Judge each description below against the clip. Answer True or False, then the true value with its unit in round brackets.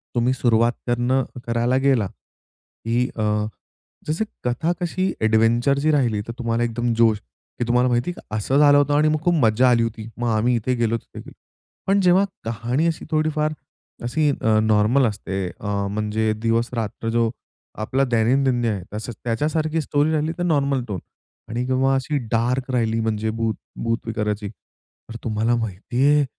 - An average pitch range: True (3.7 semitones)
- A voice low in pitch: True (120 Hz)